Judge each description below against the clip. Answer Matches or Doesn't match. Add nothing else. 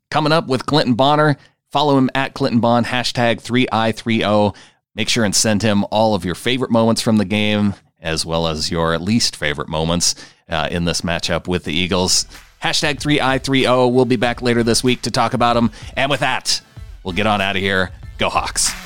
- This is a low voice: Matches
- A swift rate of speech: Matches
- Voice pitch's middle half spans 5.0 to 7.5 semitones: Matches